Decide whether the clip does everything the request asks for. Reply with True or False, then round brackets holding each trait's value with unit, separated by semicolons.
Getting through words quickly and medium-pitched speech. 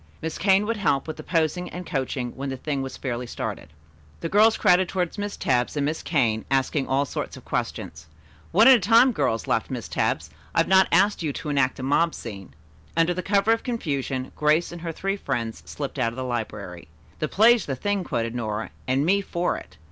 True (215 wpm; 150 Hz)